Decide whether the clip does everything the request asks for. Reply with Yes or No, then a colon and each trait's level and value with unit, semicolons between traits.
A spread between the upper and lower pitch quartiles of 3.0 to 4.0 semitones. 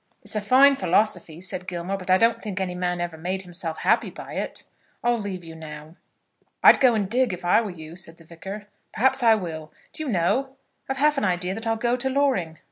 No: average, 5.1 semitones